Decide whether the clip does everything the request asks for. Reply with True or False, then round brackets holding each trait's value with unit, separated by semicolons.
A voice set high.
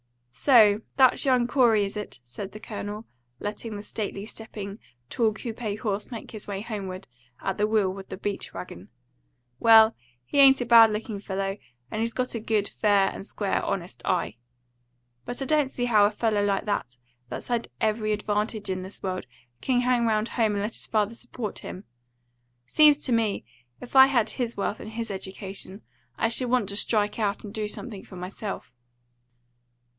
True (215 Hz)